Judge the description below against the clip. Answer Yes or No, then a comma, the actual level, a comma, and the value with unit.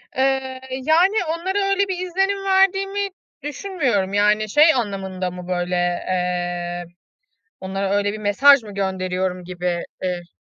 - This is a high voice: Yes, high, 205 Hz